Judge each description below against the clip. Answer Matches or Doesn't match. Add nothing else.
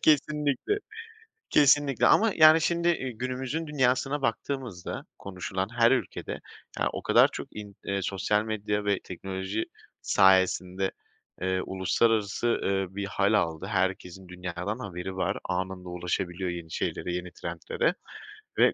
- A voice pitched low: Matches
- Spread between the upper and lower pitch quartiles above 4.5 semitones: Matches